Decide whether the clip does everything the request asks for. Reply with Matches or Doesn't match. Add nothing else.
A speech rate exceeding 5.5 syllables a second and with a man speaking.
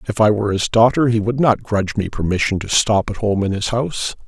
Matches